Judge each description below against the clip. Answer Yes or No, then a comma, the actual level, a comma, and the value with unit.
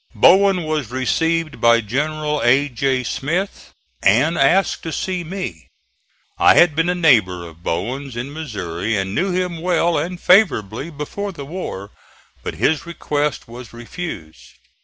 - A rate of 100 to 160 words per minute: Yes, average, 145 wpm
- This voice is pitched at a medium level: Yes, medium, 145 Hz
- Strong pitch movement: Yes, wide, 6.6 semitones